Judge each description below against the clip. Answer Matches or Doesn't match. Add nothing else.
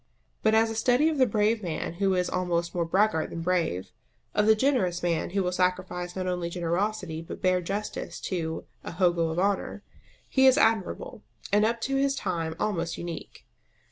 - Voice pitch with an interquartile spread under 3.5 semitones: Doesn't match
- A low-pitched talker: Doesn't match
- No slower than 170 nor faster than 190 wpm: Matches